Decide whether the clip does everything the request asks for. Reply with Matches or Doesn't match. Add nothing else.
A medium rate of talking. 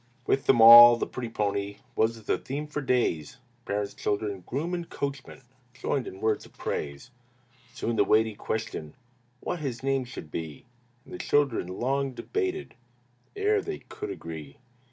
Matches